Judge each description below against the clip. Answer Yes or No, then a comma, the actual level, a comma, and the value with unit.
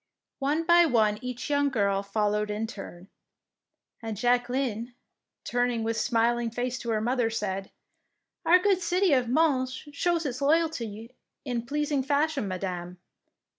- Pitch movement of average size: Yes, average, 4.7 semitones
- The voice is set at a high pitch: Yes, high, 245 Hz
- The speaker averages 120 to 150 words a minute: Yes, average, 140 wpm